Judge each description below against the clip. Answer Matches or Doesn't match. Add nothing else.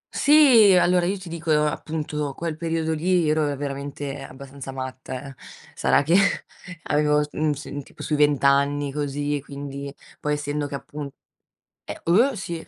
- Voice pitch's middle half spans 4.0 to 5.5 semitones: Doesn't match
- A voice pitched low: Doesn't match